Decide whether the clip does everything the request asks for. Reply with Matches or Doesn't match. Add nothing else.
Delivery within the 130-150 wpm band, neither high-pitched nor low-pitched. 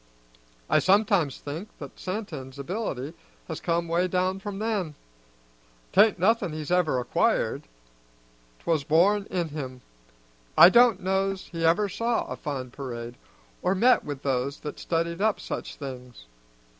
Matches